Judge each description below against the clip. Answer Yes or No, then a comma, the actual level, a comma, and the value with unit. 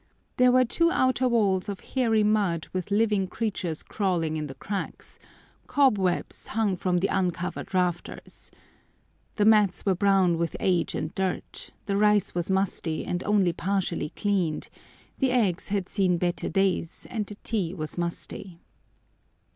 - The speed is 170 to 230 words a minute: No, average, 145 wpm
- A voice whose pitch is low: No, high, 190 Hz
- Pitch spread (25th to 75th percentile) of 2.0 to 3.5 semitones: Yes, average, 3.1 semitones